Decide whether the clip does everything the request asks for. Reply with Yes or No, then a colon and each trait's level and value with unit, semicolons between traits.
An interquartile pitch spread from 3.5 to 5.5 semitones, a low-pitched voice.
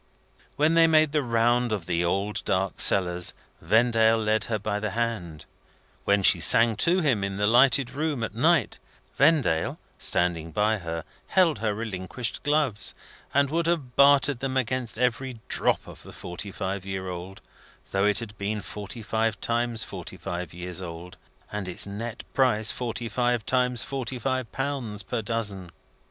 Yes: average, 4.7 semitones; low, 110 Hz